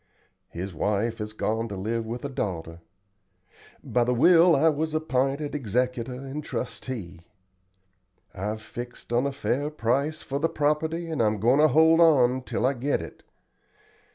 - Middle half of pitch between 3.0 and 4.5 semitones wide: No, average, 4.9 semitones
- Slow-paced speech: No, average, 155 wpm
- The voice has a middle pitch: No, low, 125 Hz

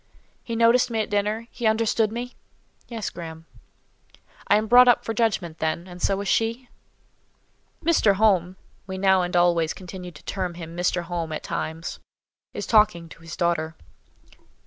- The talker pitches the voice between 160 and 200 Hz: Yes, high, 190 Hz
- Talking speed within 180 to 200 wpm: No, average, 165 wpm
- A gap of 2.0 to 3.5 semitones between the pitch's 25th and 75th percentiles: No, average, 4.6 semitones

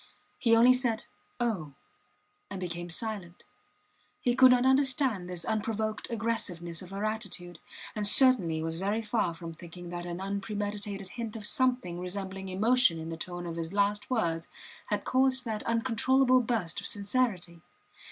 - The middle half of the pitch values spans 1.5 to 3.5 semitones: No, average, 4.9 semitones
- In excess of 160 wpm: No, average, 150 wpm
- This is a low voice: No, high, 205 Hz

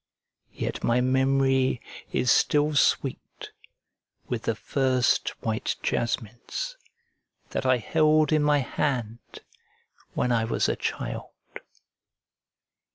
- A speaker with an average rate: No, slow, 100 wpm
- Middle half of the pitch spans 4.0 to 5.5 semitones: No, average, 3.3 semitones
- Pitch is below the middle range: Yes, low, 130 Hz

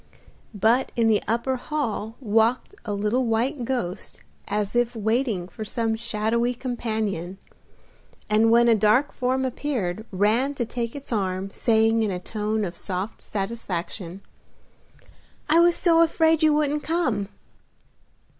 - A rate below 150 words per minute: Yes, slow, 135 wpm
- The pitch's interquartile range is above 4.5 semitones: No, average, 3.5 semitones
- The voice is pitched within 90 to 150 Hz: No, high, 225 Hz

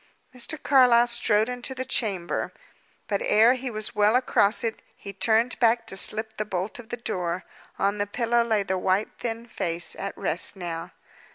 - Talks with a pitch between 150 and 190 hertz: No, high, 220 Hz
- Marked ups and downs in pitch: No, average, 3.2 semitones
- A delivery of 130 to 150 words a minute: No, average, 180 wpm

